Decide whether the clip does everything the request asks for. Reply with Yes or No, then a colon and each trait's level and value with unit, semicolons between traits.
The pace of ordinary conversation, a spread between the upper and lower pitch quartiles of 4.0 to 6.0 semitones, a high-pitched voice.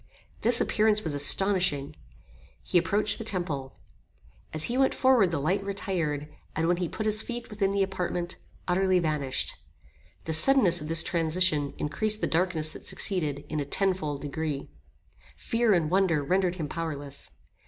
No: average, 155 wpm; average, 4.4 semitones; medium, 175 Hz